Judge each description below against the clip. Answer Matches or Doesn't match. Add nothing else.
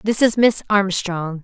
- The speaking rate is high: Doesn't match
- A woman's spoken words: Matches